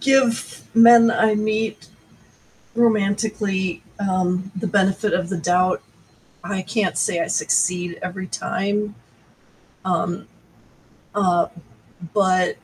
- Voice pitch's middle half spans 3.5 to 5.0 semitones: No, average, 2.9 semitones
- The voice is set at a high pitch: Yes, high, 195 Hz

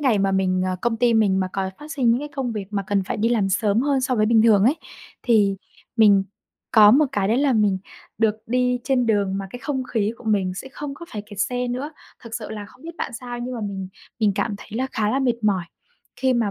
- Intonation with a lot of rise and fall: No, average, 3.8 semitones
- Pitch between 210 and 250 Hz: Yes, high, 225 Hz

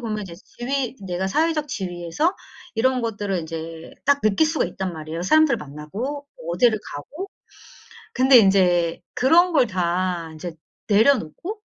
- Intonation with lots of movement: Yes, wide, 8.2 semitones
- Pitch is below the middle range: No, high, 210 Hz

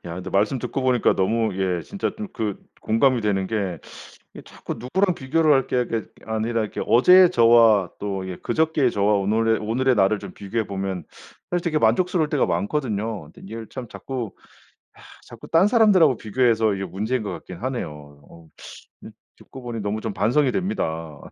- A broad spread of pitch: No, average, 4.8 semitones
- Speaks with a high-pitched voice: No, low, 115 Hz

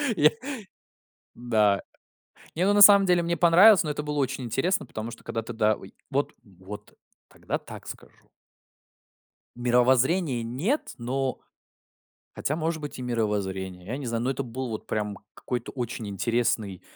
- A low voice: Yes, low, 125 Hz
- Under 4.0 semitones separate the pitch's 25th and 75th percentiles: No, wide, 5.4 semitones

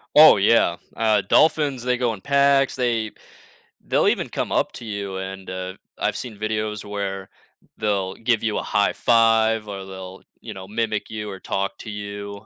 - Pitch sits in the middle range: No, low, 105 Hz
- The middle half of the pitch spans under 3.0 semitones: Yes, narrow, 2.6 semitones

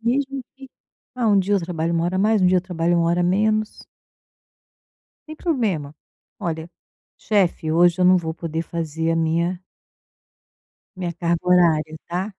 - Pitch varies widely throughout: No, average, 3.5 semitones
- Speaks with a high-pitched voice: No, medium, 175 Hz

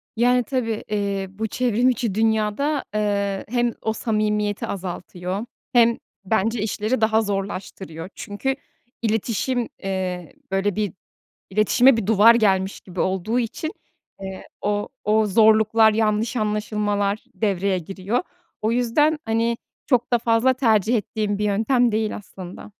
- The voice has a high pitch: Yes, high, 215 Hz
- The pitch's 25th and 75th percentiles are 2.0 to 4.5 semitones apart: Yes, narrow, 2.6 semitones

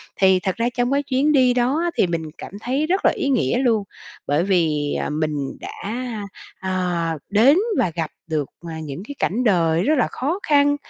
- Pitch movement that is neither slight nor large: No, wide, 8.3 semitones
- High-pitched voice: Yes, high, 195 Hz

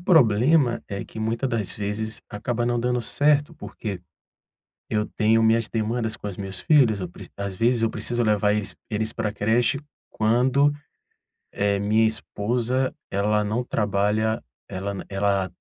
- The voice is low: Yes, low, 110 Hz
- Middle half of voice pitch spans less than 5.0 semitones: Yes, average, 2.7 semitones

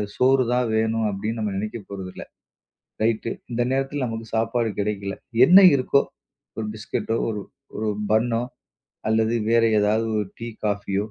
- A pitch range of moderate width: No, narrow, 1.8 semitones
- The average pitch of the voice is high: No, low, 110 Hz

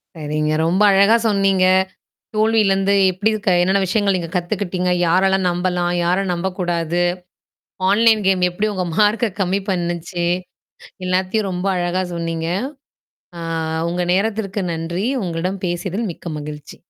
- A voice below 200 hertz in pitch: Yes, medium, 185 Hz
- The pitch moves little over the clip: Yes, narrow, 2.2 semitones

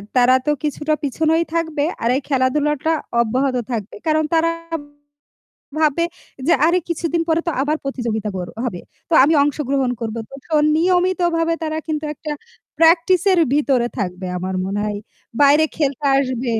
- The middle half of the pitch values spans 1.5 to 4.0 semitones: No, average, 4.5 semitones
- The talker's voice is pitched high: Yes, very high, 295 Hz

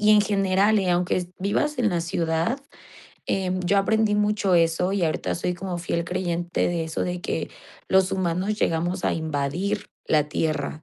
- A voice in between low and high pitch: Yes, medium, 180 Hz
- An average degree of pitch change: Yes, average, 3.0 semitones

